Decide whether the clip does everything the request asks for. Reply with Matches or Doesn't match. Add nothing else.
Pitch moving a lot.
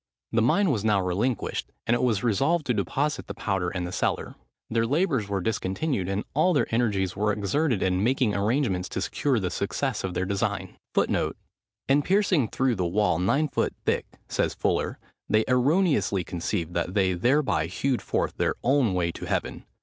Matches